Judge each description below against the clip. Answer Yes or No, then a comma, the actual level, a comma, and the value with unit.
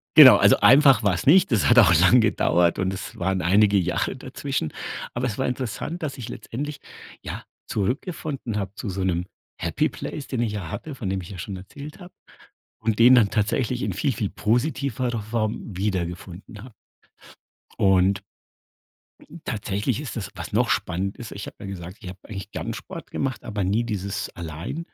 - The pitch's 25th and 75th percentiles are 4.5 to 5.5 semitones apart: Yes, average, 4.8 semitones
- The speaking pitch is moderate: No, low, 105 Hz